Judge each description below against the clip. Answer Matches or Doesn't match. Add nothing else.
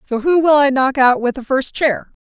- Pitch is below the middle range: Doesn't match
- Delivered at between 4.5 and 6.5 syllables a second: Matches